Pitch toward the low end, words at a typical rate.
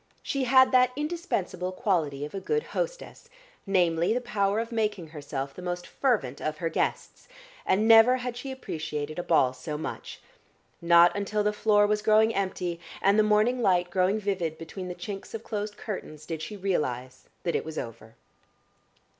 No: high, 195 Hz; average, 175 wpm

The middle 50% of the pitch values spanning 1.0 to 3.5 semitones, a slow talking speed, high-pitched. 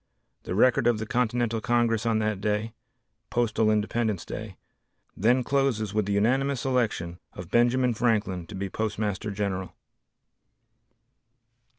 No: narrow, 2.6 semitones; slow, 125 wpm; low, 110 Hz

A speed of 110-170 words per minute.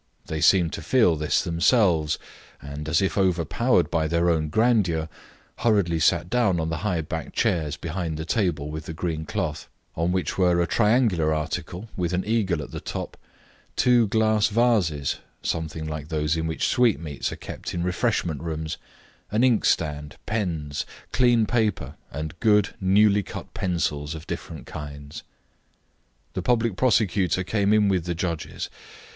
Yes: average, 155 wpm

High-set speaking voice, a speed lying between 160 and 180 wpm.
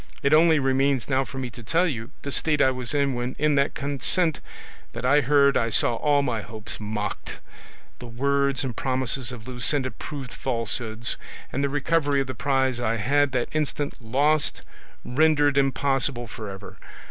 No: low, 135 Hz; average, 175 wpm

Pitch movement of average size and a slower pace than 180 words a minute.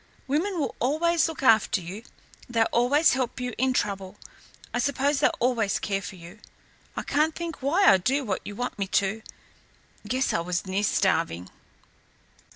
No: wide, 6.3 semitones; average, 160 wpm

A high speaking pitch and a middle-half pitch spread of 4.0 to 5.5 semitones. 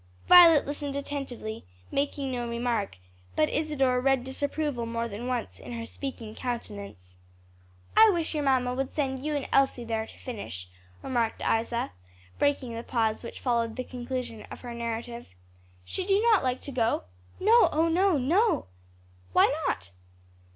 No: very high, 250 Hz; average, 3.6 semitones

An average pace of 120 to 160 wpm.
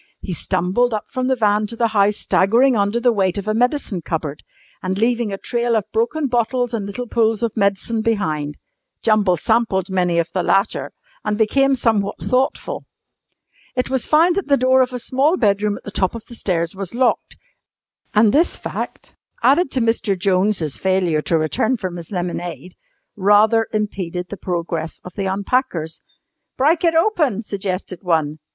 No: average, 175 wpm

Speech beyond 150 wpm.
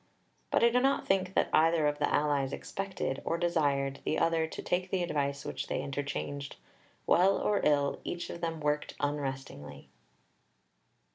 Yes: average, 160 wpm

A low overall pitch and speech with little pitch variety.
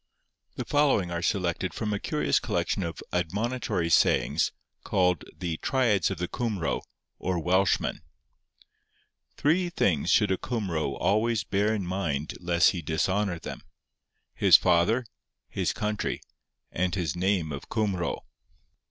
No: very low, 95 Hz; average, 3.7 semitones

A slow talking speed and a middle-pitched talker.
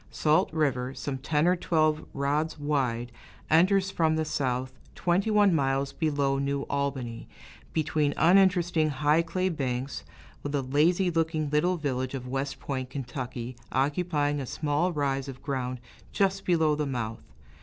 No: average, 145 wpm; medium, 145 Hz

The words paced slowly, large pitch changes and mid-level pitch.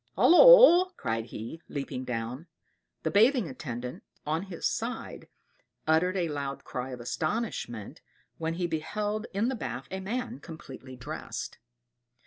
Yes: slow, 130 wpm; wide, 8.6 semitones; medium, 160 Hz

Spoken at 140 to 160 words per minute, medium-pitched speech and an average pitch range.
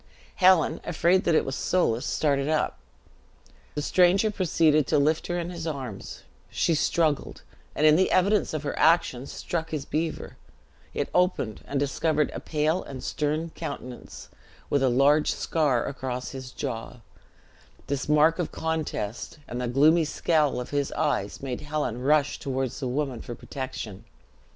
Yes: average, 155 wpm; medium, 150 Hz; average, 3.6 semitones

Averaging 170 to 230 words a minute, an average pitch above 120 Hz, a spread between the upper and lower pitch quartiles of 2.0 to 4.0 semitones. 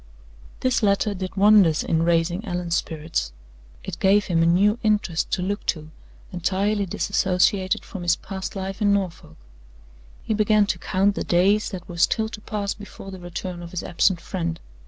Yes: average, 175 wpm; high, 190 Hz; average, 2.9 semitones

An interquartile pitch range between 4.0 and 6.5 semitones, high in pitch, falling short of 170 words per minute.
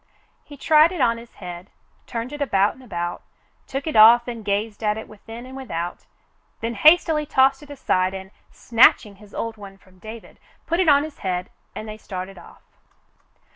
No: wide, 5.4 semitones; high, 225 Hz; average, 185 wpm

